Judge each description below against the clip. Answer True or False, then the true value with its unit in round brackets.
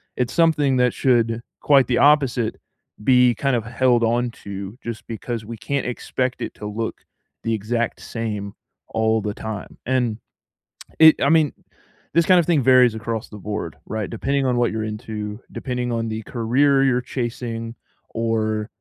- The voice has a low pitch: True (120 Hz)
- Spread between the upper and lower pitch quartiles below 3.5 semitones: True (2.7 semitones)